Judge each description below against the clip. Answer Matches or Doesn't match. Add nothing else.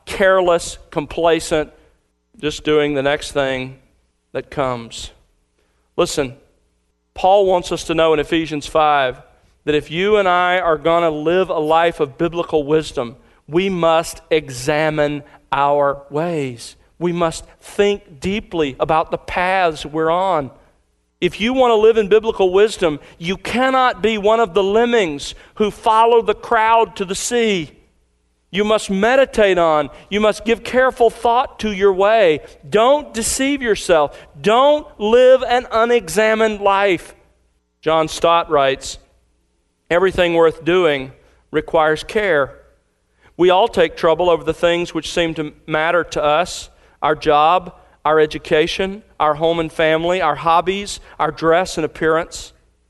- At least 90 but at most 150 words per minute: Matches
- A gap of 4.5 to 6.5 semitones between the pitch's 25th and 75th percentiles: Matches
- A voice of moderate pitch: Matches